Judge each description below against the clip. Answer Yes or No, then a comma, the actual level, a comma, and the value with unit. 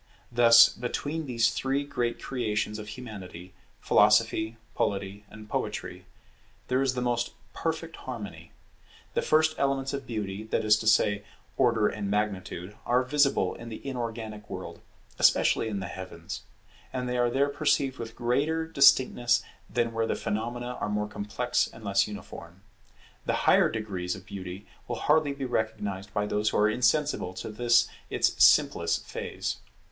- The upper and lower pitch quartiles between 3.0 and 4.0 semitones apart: Yes, average, 3.5 semitones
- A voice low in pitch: Yes, low, 115 Hz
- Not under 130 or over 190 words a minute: Yes, average, 155 wpm